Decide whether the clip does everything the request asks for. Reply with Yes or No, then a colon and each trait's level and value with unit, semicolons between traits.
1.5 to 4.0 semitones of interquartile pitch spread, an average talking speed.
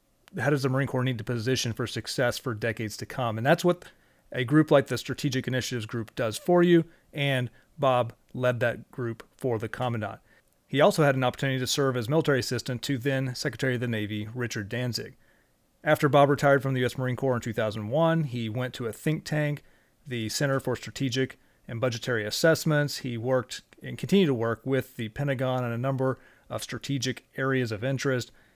Yes: narrow, 2.6 semitones; average, 195 wpm